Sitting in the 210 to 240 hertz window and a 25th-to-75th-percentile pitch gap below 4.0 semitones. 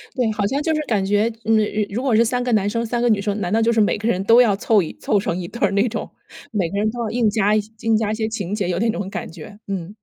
Yes: high, 215 Hz; narrow, 2.5 semitones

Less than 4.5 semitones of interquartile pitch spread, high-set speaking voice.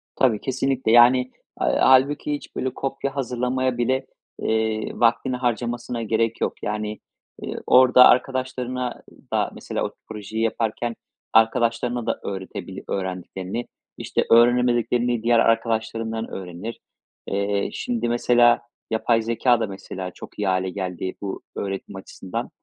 No: average, 2.7 semitones; low, 115 Hz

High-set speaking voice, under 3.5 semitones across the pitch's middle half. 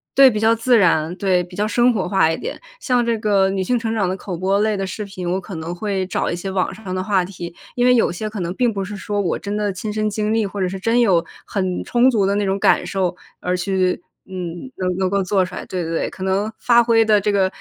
Yes: high, 195 Hz; average, 2.8 semitones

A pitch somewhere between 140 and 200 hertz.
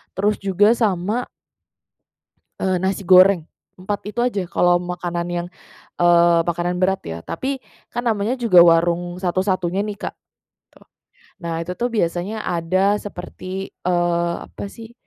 Yes: medium, 185 Hz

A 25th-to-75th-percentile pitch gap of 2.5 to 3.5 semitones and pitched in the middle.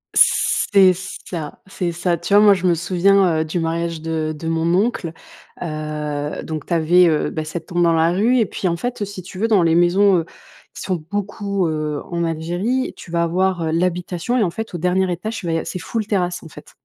Yes: average, 2.9 semitones; medium, 175 Hz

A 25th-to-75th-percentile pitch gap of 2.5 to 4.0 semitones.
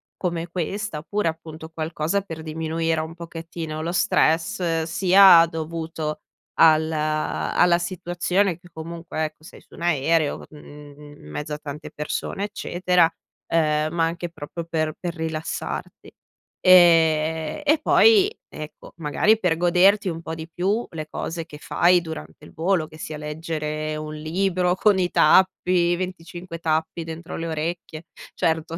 No: narrow, 2.1 semitones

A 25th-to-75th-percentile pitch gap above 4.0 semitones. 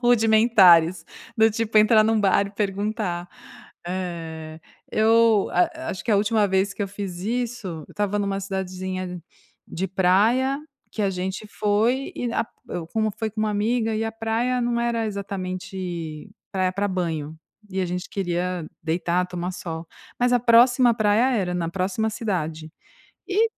No: average, 3.6 semitones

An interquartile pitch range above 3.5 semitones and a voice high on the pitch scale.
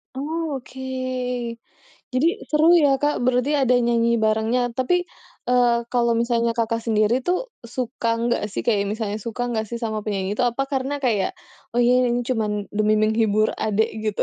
No: average, 2.9 semitones; high, 235 Hz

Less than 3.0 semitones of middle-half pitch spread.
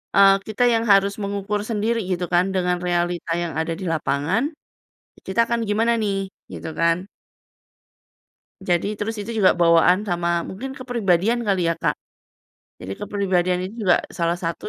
No: average, 3.3 semitones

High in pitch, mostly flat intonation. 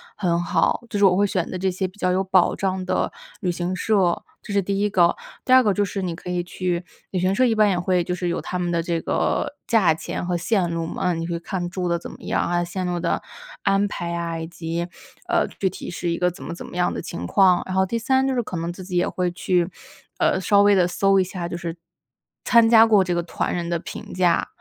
No: medium, 180 Hz; narrow, 2.2 semitones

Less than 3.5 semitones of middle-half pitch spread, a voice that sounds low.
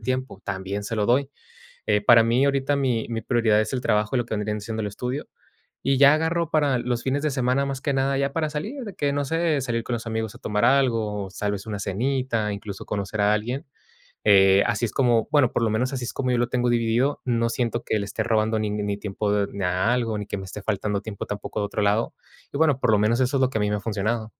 No: average, 4.2 semitones; low, 115 Hz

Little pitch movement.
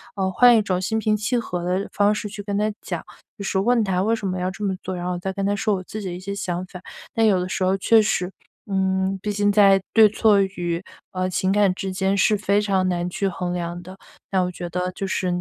Yes: narrow, 2.1 semitones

